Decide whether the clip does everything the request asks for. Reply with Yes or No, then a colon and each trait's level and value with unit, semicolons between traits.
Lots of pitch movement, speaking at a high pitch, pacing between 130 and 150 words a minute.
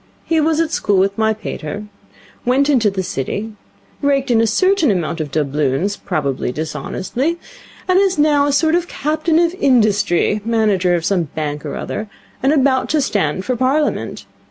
No: wide, 8.5 semitones; high, 225 Hz; average, 170 wpm